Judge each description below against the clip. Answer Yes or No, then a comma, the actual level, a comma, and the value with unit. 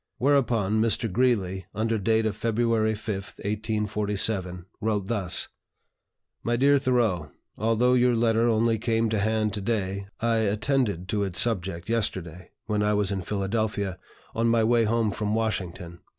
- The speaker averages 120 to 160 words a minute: Yes, average, 150 wpm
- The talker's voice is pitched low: Yes, low, 110 Hz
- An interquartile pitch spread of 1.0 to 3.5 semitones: Yes, average, 2.7 semitones